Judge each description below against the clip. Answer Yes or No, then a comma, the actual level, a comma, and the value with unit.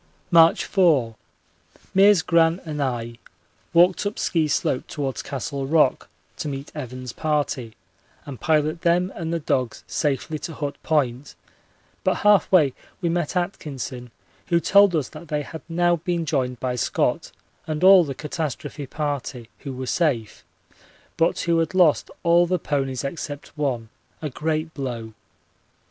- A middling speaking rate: Yes, average, 150 wpm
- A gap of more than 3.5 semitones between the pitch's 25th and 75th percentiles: Yes, average, 4.1 semitones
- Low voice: No, medium, 150 Hz